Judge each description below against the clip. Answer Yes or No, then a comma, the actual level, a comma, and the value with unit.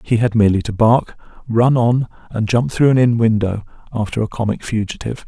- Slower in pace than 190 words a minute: No, average, 195 wpm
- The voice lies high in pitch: No, low, 115 Hz